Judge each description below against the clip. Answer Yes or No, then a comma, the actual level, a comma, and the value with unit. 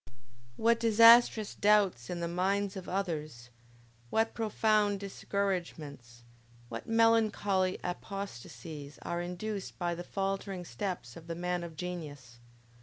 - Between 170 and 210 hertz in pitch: Yes, medium, 185 Hz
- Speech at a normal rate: No, slow, 115 wpm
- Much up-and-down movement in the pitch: No, average, 3.9 semitones